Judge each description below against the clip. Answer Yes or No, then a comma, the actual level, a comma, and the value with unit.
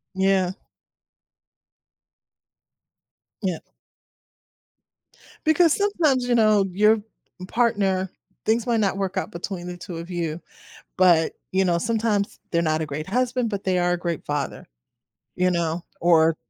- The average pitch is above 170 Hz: Yes, high, 190 Hz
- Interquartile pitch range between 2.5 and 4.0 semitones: No, average, 4.4 semitones